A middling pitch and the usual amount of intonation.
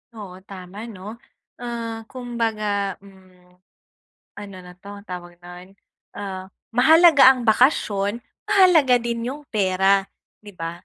No: high, 205 Hz; average, 4.2 semitones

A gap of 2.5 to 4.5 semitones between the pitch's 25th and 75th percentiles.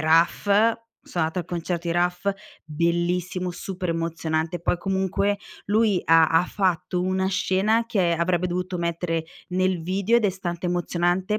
No: narrow, 1.9 semitones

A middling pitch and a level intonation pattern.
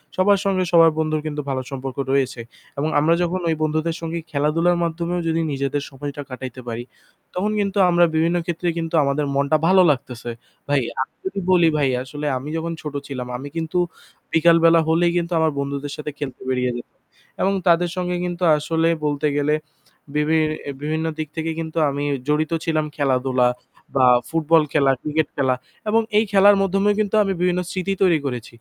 No: medium, 155 Hz; average, 3.5 semitones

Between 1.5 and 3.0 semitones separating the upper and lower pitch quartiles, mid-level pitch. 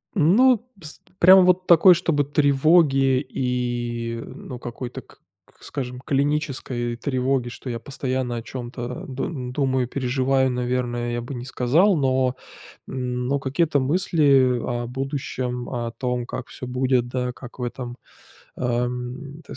No: narrow, 2.4 semitones; low, 130 Hz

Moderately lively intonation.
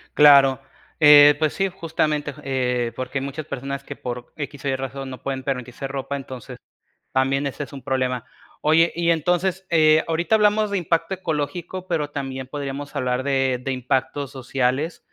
Yes: average, 3.3 semitones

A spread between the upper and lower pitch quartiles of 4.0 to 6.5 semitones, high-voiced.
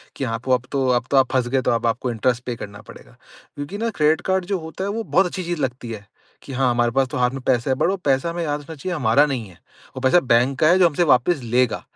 No: average, 4.8 semitones; low, 135 Hz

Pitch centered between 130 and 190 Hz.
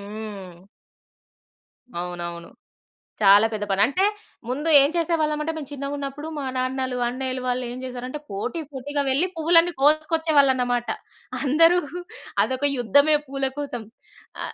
No: very high, 265 Hz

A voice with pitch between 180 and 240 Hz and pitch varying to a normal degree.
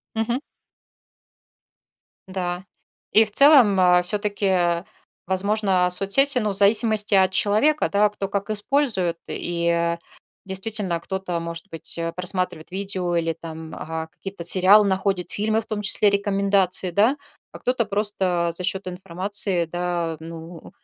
Yes: high, 190 Hz; average, 3.0 semitones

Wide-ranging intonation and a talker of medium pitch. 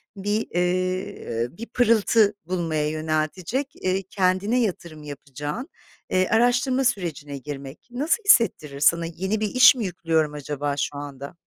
Yes: wide, 6.6 semitones; medium, 180 Hz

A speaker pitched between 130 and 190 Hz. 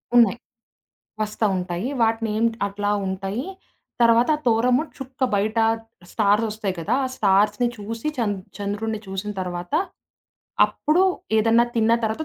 No: high, 220 Hz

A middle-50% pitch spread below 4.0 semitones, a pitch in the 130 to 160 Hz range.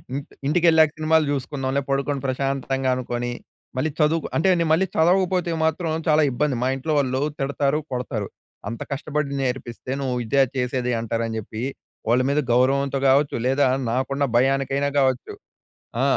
Yes: average, 2.8 semitones; low, 135 Hz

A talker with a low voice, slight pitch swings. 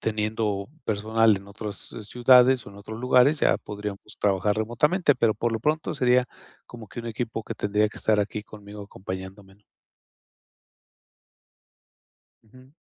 No: low, 110 Hz; average, 3.0 semitones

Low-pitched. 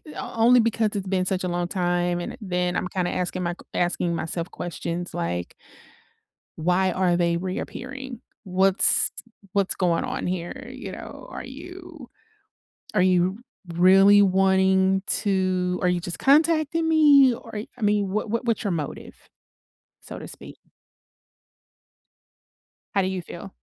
No: high, 190 Hz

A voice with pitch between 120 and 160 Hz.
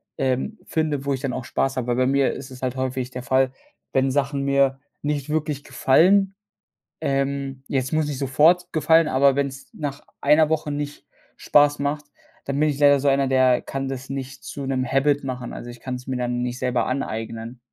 Yes: low, 135 Hz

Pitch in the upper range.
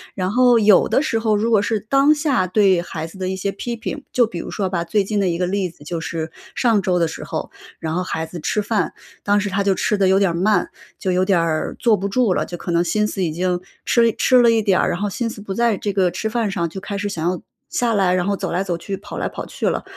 Yes: high, 195 Hz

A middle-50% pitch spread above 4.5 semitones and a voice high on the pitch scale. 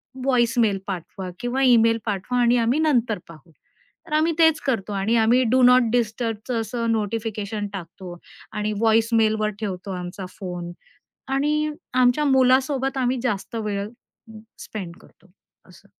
No: average, 3.7 semitones; high, 225 Hz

